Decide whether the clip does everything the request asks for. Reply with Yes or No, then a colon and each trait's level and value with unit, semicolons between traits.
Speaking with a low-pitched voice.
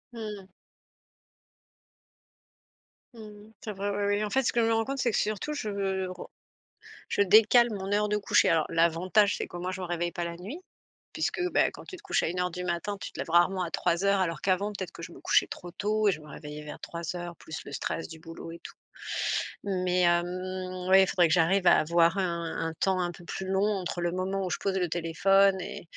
No: medium, 185 Hz